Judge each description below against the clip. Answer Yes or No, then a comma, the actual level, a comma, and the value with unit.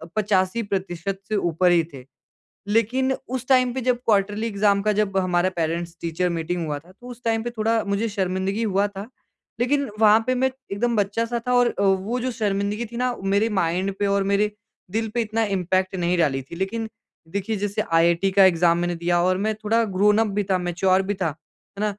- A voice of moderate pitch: No, high, 200 Hz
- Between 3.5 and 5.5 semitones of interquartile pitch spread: Yes, average, 3.8 semitones